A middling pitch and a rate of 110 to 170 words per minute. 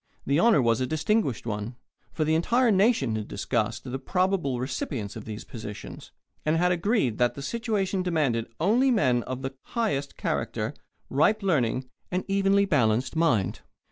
Yes: medium, 145 Hz; average, 160 wpm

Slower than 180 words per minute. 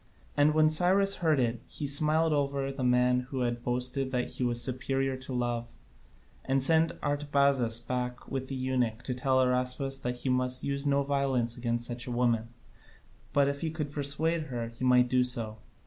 No: average, 185 wpm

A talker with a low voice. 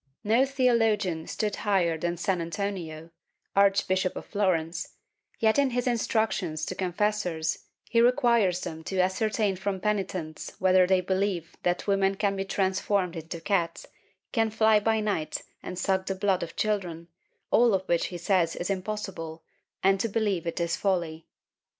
No: high, 190 Hz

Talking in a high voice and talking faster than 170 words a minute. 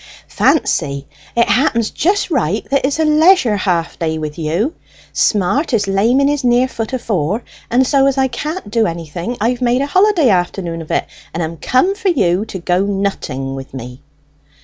Yes: high, 220 Hz; average, 190 wpm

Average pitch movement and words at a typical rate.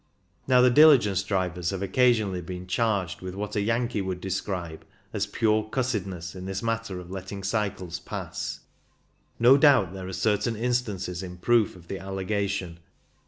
Yes: average, 3.7 semitones; average, 160 wpm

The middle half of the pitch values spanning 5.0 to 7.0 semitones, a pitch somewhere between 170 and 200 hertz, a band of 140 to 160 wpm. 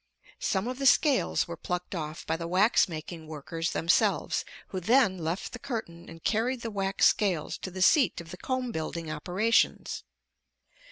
No: wide, 5.6 semitones; medium, 185 Hz; average, 170 wpm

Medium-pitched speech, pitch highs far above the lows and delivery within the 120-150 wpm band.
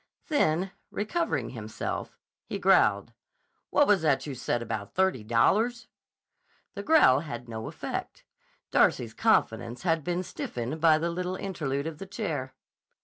Yes: medium, 165 Hz; wide, 6.8 semitones; average, 140 wpm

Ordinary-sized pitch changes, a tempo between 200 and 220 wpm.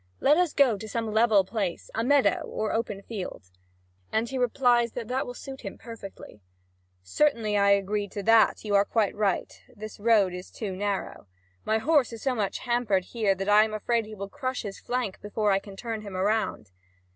Yes: average, 3.1 semitones; fast, 205 wpm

